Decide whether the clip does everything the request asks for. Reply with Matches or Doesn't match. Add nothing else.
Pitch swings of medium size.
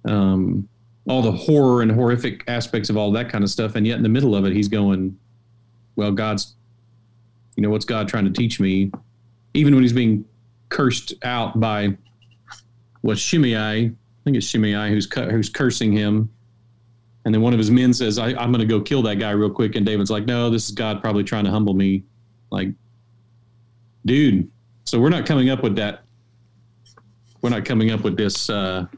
Doesn't match